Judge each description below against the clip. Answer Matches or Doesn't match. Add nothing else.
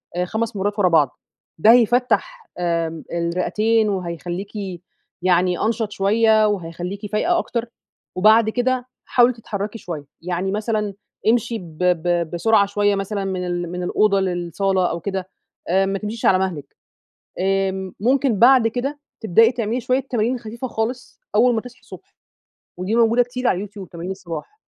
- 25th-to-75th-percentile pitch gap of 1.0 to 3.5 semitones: Doesn't match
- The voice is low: Doesn't match